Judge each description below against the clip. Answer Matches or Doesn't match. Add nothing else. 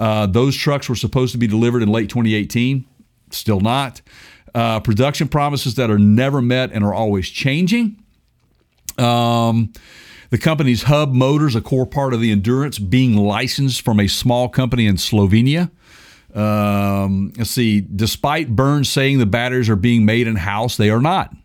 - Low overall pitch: Matches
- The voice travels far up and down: Doesn't match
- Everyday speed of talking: Matches